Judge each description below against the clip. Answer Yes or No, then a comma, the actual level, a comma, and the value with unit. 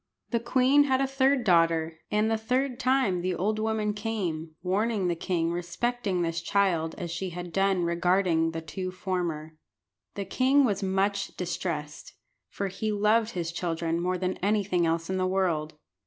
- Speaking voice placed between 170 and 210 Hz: Yes, medium, 185 Hz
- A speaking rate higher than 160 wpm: Yes, average, 170 wpm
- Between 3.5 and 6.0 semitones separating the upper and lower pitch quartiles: Yes, average, 4.1 semitones